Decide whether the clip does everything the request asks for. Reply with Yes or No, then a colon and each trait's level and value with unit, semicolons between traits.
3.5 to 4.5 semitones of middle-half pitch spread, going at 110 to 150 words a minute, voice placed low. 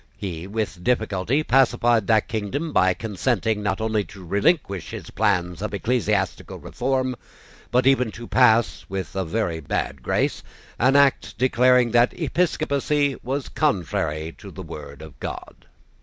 No: average, 5.1 semitones; average, 140 wpm; low, 110 Hz